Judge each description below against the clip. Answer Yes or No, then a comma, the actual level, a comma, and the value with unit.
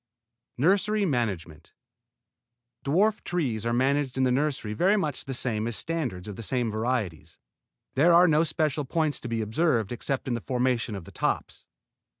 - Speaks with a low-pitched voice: Yes, low, 130 Hz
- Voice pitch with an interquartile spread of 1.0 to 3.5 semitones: No, wide, 5.6 semitones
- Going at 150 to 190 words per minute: Yes, average, 165 wpm